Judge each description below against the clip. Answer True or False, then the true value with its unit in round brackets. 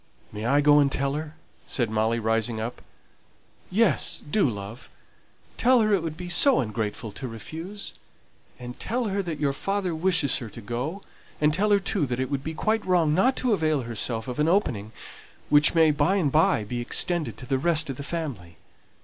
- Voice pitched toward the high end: False (150 Hz)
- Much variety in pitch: True (7.0 semitones)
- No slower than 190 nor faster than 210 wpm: True (195 wpm)